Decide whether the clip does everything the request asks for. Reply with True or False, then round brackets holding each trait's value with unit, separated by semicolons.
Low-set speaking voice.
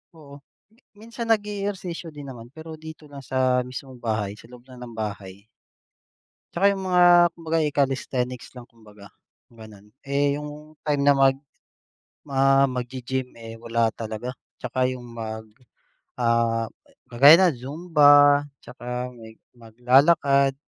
True (130 Hz)